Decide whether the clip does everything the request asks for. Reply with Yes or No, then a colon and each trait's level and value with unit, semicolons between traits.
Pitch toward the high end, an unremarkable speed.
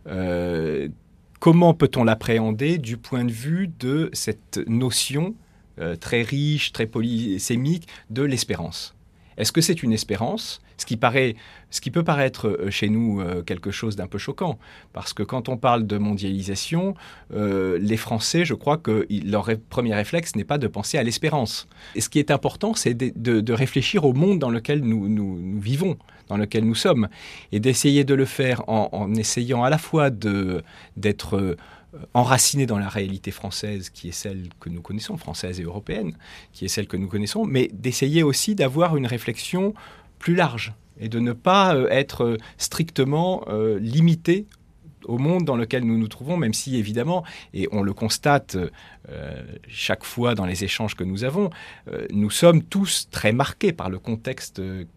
No: low, 115 Hz; average, 180 wpm